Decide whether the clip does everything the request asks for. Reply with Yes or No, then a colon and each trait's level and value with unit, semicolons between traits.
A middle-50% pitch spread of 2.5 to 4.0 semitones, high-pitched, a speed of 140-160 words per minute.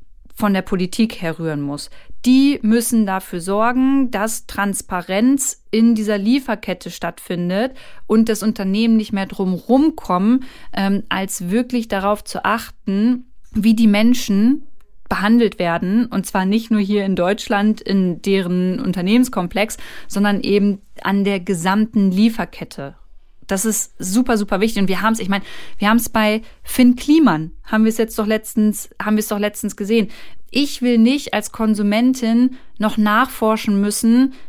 Yes: average, 2.8 semitones; high, 215 Hz; average, 150 wpm